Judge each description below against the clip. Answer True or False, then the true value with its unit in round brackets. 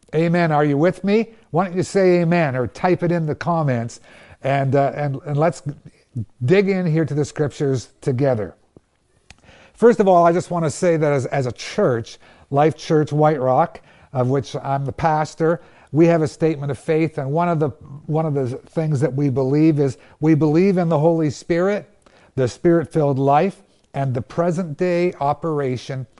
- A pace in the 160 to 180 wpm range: False (190 wpm)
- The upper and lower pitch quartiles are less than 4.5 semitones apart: True (3.6 semitones)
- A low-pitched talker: False (155 Hz)